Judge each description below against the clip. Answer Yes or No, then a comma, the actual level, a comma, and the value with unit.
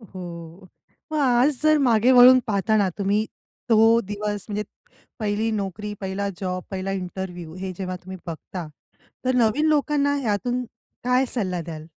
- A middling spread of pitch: Yes, average, 4.6 semitones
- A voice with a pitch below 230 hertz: Yes, high, 205 Hz